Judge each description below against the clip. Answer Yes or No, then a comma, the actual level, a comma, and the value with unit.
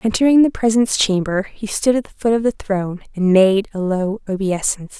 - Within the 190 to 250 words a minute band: Yes, fast, 205 wpm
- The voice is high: Yes, high, 205 Hz